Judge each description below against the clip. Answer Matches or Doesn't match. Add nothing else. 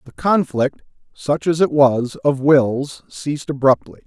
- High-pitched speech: Doesn't match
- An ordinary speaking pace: Matches